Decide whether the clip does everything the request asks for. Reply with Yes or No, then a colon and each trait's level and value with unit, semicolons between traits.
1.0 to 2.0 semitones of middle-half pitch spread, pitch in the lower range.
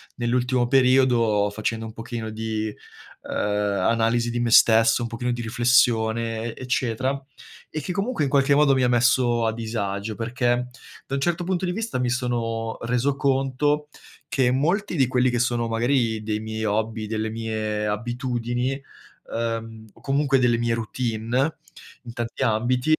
No: narrow, 2.5 semitones; low, 120 Hz